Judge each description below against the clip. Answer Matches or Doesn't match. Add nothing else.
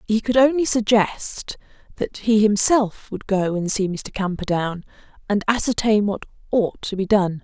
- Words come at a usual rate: Matches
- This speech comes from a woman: Matches